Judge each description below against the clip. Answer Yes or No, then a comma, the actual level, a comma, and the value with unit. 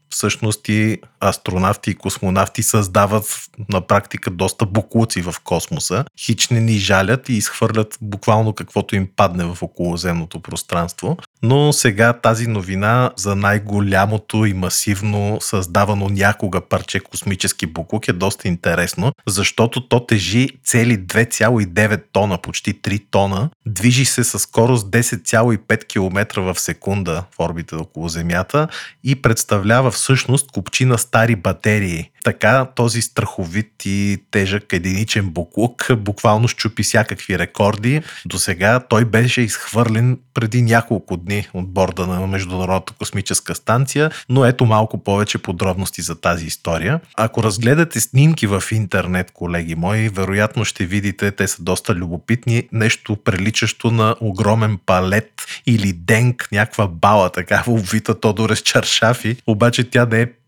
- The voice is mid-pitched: No, low, 105 Hz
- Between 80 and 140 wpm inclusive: Yes, average, 130 wpm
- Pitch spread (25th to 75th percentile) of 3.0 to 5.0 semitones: Yes, average, 3.3 semitones